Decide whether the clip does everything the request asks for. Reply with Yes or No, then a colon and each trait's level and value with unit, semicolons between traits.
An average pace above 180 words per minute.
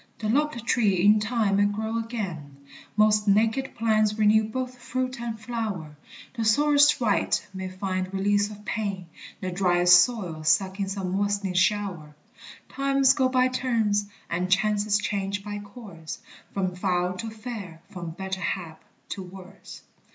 No: average, 150 wpm